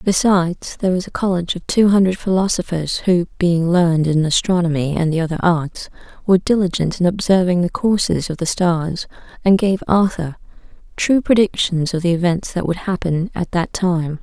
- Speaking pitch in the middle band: Yes, medium, 175 Hz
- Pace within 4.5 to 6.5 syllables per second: Yes, 5.2 syllables/s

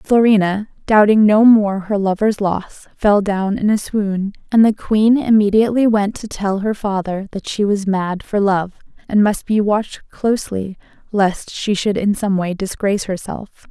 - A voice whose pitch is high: Yes, high, 205 Hz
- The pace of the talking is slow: No, average, 175 wpm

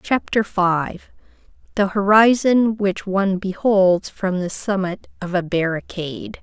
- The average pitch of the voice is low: No, high, 195 Hz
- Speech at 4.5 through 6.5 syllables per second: No, 4.0 syllables/s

